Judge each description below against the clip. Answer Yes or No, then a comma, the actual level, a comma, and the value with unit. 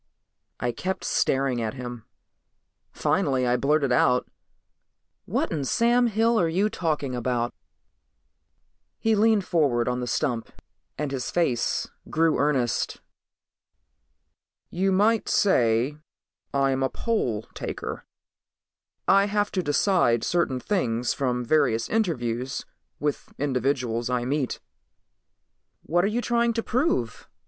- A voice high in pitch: No, medium, 140 Hz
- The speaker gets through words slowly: Yes, slow, 120 wpm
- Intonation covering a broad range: Yes, wide, 7.6 semitones